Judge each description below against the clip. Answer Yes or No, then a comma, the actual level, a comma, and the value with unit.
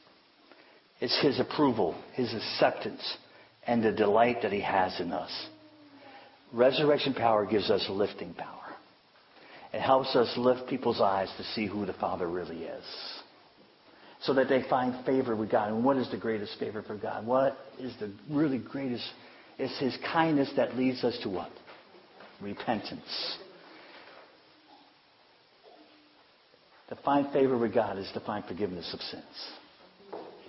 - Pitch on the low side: Yes, low, 130 Hz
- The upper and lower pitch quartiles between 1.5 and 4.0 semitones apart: Yes, average, 3.3 semitones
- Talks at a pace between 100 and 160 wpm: Yes, average, 140 wpm